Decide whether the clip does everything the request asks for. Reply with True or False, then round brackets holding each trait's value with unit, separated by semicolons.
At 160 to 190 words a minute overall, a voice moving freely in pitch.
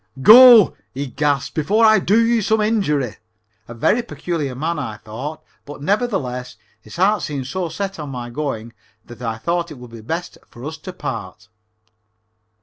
True (170 wpm; 7.8 semitones)